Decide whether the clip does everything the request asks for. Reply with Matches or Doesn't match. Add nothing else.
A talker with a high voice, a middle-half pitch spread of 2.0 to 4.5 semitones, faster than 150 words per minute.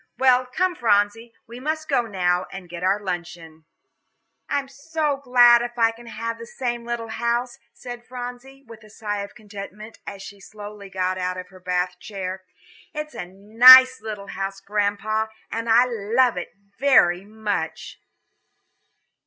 Matches